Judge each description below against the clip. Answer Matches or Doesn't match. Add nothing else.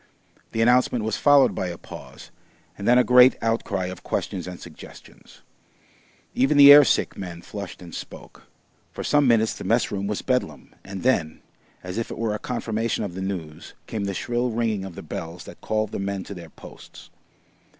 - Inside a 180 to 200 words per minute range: Matches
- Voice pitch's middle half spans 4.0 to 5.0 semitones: Matches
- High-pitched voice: Doesn't match